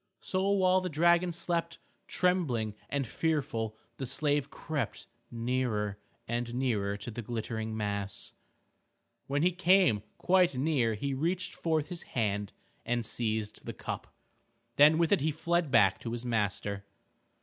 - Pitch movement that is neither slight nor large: No, wide, 7.1 semitones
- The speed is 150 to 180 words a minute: No, average, 140 wpm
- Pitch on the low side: Yes, low, 130 Hz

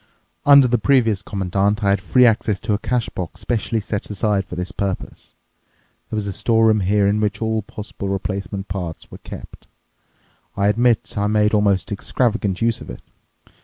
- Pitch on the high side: No, low, 105 Hz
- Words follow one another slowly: No, average, 180 wpm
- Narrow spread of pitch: Yes, narrow, 2.2 semitones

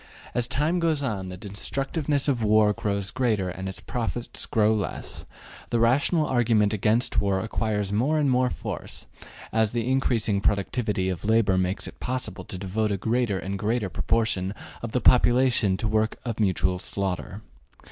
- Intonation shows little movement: No, average, 3.9 semitones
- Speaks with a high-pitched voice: No, low, 110 Hz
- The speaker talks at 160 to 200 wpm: Yes, average, 165 wpm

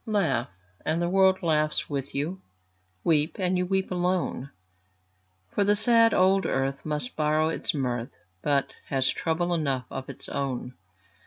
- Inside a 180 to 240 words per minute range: No, average, 150 wpm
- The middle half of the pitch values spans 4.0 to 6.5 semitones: Yes, average, 5.1 semitones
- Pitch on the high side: No, medium, 160 Hz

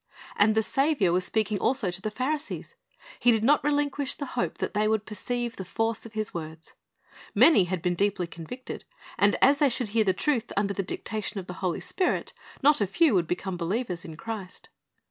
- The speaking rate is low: No, fast, 205 wpm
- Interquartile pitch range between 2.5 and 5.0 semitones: No, wide, 5.4 semitones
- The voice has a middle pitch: No, high, 215 Hz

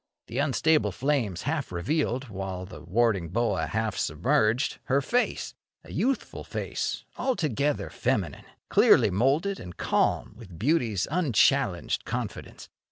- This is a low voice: Yes, low, 120 Hz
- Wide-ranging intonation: Yes, wide, 7.3 semitones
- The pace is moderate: No, slow, 120 wpm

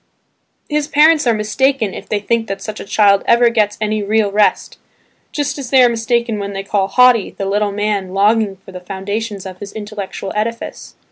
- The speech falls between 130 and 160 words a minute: No, average, 195 wpm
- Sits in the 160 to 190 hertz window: No, high, 210 Hz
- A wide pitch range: No, average, 2.7 semitones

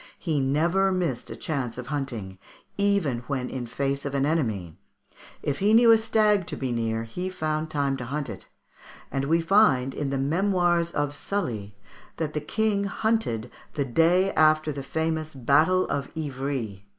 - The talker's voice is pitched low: No, medium, 150 Hz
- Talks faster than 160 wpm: Yes, average, 175 wpm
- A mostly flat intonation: No, average, 5.0 semitones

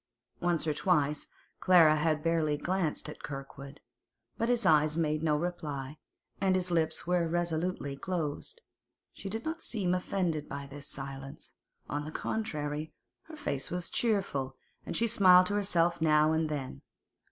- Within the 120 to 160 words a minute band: Yes, average, 150 wpm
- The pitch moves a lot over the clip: No, average, 3.6 semitones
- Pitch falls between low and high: Yes, medium, 160 Hz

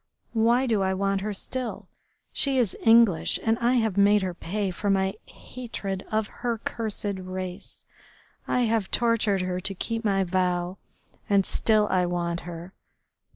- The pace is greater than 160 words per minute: No, average, 155 wpm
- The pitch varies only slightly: No, average, 3.4 semitones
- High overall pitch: Yes, high, 200 Hz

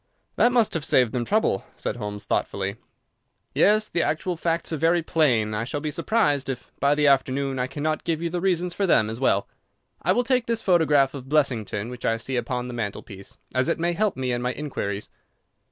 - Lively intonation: Yes, wide, 5.8 semitones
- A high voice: No, medium, 140 Hz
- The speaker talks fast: Yes, fast, 215 wpm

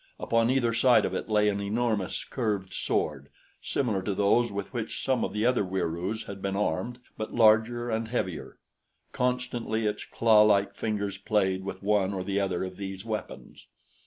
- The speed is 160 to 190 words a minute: Yes, average, 170 wpm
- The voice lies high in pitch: No, low, 105 Hz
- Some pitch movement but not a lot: Yes, average, 3.0 semitones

